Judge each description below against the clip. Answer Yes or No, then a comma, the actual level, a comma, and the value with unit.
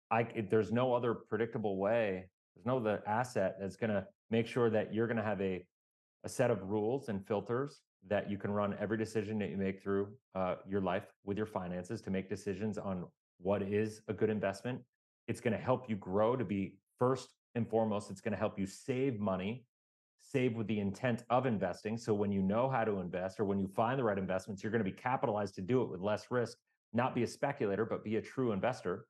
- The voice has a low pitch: Yes, low, 105 Hz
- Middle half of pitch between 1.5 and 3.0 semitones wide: Yes, average, 2.7 semitones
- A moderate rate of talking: No, fast, 225 wpm